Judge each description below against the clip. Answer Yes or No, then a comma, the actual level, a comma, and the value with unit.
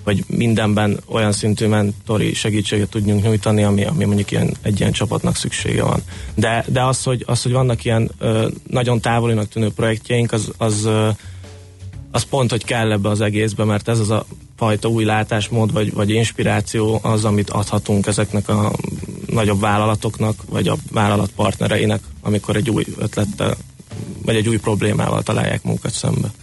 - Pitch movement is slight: Yes, narrow, 1.7 semitones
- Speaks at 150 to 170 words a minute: Yes, fast, 155 wpm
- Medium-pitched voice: No, low, 110 Hz